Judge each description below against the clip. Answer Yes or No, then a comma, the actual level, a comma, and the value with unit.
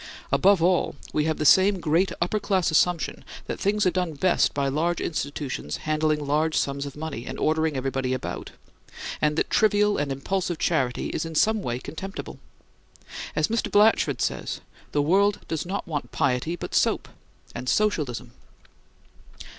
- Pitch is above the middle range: No, medium, 160 Hz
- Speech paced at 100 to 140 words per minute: No, average, 155 wpm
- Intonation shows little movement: No, average, 4.8 semitones